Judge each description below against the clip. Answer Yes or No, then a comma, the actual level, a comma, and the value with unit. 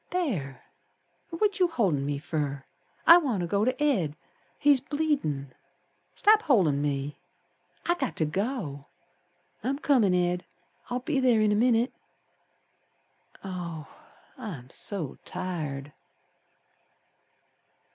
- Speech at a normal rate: No, slow, 115 wpm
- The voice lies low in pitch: No, high, 200 Hz